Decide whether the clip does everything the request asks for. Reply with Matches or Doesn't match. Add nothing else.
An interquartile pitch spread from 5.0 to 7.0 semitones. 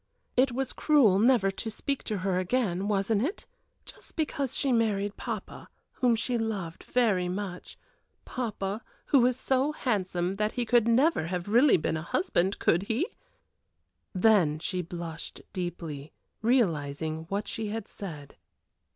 Matches